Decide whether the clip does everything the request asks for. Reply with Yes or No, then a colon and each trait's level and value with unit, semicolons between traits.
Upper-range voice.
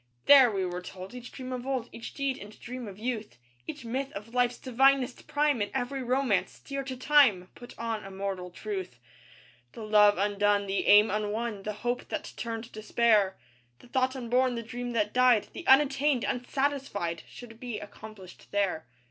Yes: high, 230 Hz